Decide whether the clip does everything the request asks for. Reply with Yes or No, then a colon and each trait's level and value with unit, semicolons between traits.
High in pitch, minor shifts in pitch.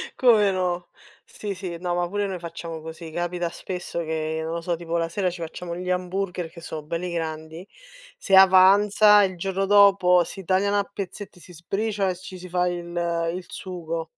No: medium, 180 Hz; narrow, 2.3 semitones